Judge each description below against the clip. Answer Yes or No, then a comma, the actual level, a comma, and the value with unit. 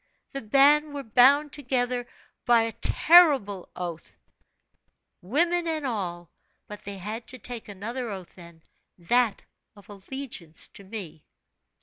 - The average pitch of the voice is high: Yes, high, 230 Hz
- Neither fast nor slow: No, slow, 125 wpm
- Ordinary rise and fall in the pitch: No, wide, 6.1 semitones